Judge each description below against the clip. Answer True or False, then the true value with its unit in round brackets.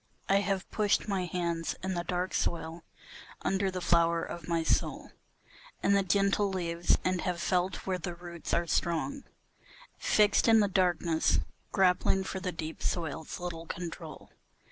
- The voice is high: False (180 Hz)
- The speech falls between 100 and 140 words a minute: False (155 wpm)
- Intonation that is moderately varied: False (2.2 semitones)